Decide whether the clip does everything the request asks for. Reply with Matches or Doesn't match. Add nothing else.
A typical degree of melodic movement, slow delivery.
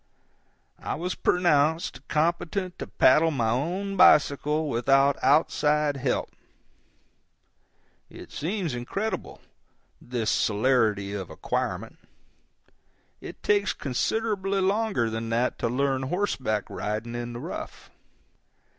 Doesn't match